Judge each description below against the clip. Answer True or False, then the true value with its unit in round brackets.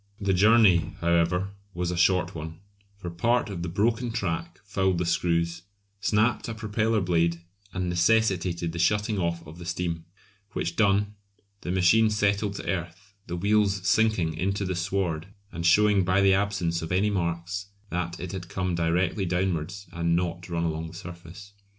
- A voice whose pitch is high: False (90 Hz)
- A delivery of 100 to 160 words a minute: False (170 wpm)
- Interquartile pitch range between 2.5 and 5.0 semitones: True (3.0 semitones)